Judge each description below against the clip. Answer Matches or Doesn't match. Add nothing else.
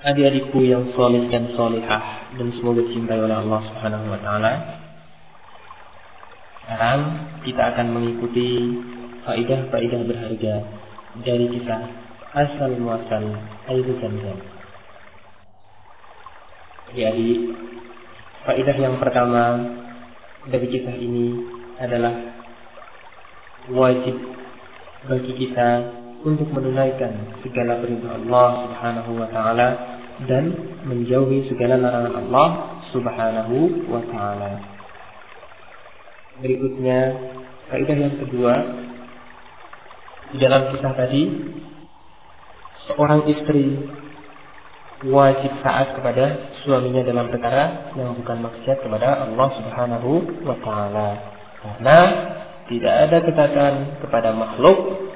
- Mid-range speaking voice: Doesn't match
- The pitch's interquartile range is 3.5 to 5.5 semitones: Doesn't match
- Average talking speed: Doesn't match